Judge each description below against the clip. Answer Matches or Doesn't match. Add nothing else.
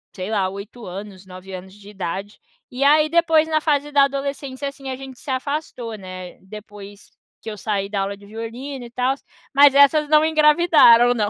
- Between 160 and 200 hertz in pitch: Doesn't match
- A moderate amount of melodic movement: Doesn't match